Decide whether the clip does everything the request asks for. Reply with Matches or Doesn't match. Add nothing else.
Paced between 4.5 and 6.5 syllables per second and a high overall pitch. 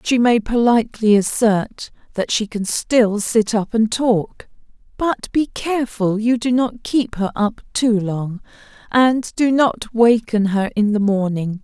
Doesn't match